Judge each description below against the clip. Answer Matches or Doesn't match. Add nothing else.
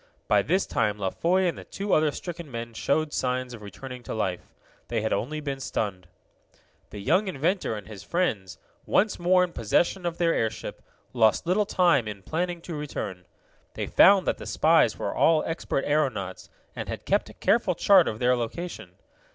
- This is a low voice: Doesn't match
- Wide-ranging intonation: Matches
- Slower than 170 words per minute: Doesn't match